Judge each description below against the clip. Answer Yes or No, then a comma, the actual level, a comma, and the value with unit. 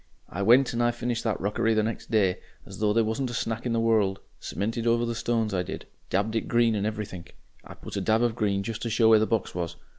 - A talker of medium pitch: No, low, 110 Hz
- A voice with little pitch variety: Yes, narrow, 2.3 semitones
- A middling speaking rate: No, fast, 250 wpm